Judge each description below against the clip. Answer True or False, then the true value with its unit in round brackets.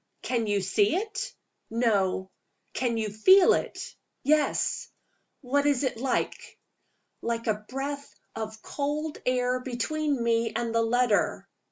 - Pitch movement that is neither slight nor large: True (4.2 semitones)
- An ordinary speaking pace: False (130 wpm)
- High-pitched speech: True (245 Hz)